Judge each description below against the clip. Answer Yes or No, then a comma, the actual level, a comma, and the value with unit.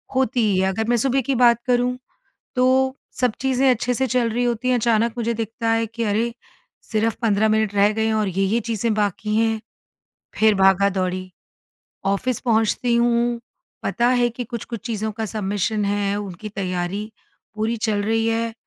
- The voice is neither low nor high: No, high, 225 Hz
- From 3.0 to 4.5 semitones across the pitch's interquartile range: No, narrow, 2.5 semitones